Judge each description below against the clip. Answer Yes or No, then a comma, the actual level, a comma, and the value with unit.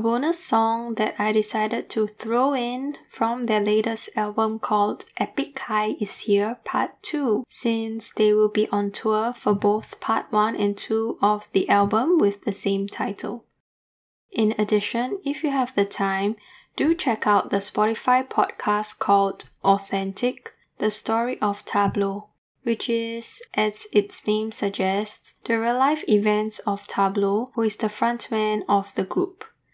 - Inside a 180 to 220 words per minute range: No, average, 155 wpm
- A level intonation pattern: Yes, narrow, 2.2 semitones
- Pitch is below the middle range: No, high, 215 Hz